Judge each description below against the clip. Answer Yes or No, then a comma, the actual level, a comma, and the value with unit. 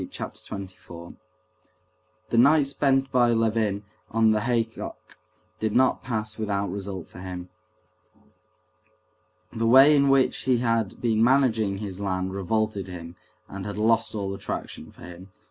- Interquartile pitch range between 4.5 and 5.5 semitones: No, average, 3.4 semitones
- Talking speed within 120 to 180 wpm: Yes, average, 140 wpm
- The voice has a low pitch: Yes, low, 110 Hz